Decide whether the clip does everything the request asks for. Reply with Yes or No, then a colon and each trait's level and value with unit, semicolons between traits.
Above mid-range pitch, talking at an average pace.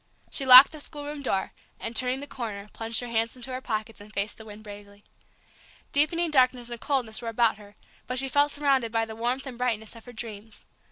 No: high, 235 Hz; fast, 215 wpm